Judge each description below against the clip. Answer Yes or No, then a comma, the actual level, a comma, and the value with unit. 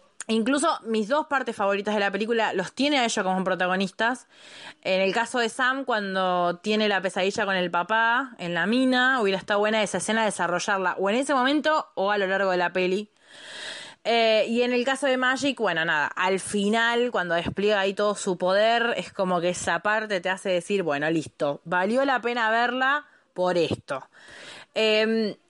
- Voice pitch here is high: Yes, high, 210 Hz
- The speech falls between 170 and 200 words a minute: Yes, fast, 190 wpm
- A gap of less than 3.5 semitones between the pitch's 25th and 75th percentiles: No, average, 4.2 semitones